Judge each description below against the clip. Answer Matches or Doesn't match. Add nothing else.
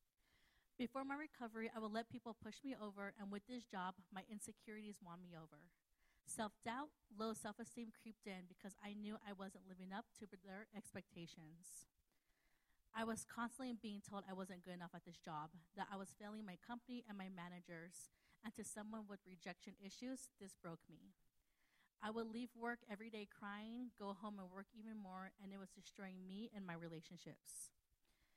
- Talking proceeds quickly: Doesn't match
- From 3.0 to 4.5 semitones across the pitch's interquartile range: Matches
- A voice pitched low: Doesn't match